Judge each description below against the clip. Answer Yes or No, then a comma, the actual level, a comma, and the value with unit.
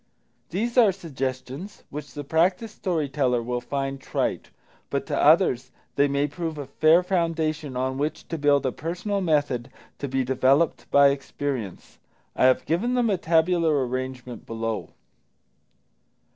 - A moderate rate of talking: Yes, average, 145 wpm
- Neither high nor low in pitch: Yes, medium, 145 Hz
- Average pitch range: Yes, average, 4.3 semitones